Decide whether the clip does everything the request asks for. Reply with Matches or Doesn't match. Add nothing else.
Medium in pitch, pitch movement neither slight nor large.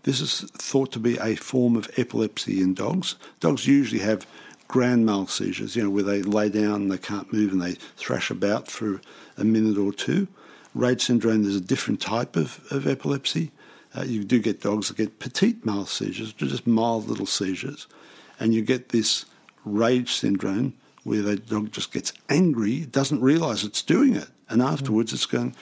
Doesn't match